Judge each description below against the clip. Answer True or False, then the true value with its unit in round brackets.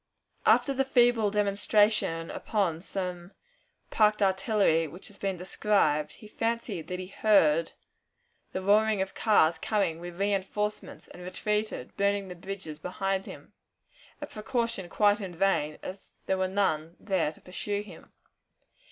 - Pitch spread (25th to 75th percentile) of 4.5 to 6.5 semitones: False (3.1 semitones)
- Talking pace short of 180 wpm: True (140 wpm)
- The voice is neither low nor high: False (195 Hz)